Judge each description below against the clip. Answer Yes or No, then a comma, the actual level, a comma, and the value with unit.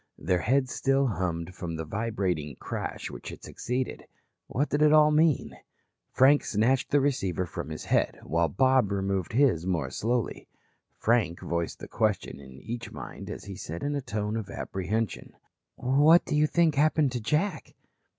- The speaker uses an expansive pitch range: Yes, wide, 7.3 semitones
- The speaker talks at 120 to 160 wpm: No, average, 170 wpm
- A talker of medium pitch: No, low, 115 Hz